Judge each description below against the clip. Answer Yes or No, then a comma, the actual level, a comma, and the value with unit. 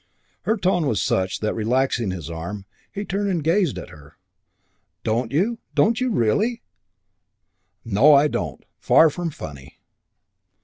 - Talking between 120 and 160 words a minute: Yes, average, 140 wpm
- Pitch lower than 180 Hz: Yes, low, 135 Hz